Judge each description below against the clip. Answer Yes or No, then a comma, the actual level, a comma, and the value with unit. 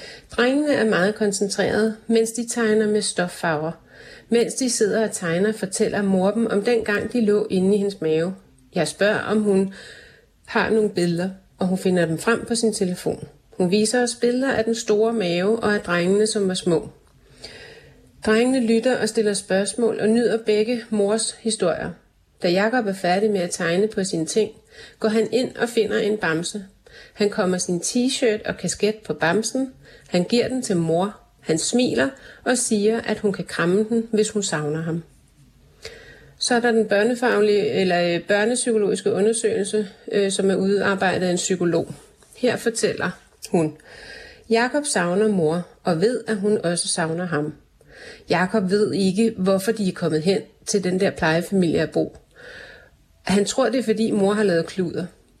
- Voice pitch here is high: Yes, high, 210 Hz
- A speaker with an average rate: Yes, average, 170 wpm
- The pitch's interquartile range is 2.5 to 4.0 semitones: Yes, average, 3.7 semitones